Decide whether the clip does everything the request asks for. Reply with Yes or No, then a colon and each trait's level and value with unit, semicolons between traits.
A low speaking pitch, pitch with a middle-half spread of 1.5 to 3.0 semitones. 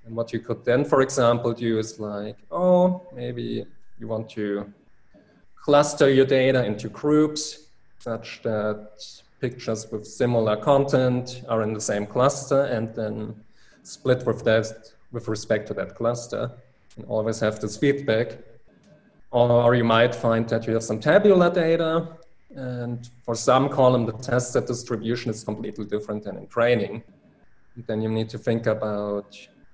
Yes: low, 115 Hz; average, 2.7 semitones